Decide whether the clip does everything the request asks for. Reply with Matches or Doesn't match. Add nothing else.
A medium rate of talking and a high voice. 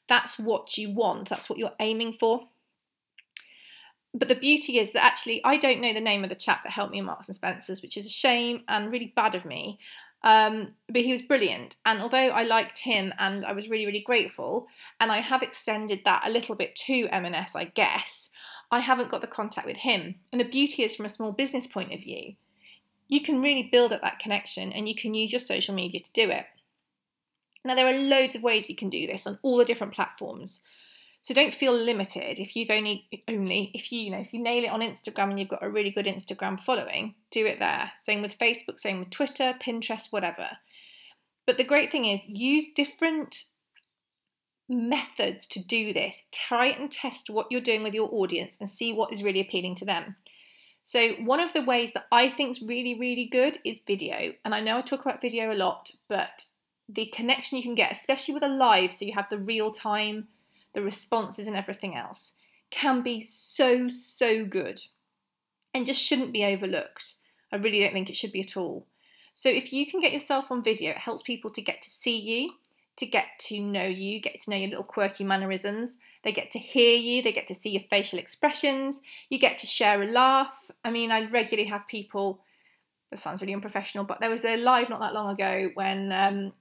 Doesn't match